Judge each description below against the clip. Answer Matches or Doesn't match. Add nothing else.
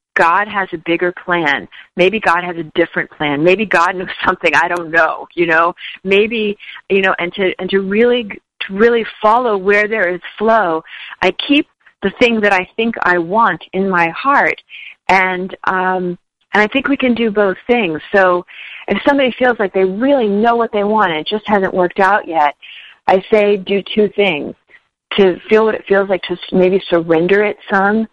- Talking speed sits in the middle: Matches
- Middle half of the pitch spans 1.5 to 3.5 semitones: Matches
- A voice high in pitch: Matches